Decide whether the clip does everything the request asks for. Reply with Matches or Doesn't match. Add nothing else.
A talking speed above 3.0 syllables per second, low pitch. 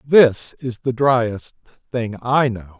Doesn't match